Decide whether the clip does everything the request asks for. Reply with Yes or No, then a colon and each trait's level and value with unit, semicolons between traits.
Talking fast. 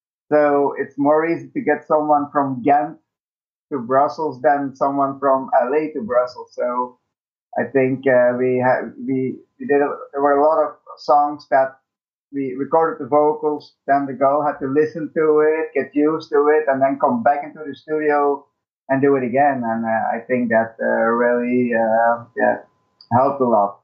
No: average, 185 wpm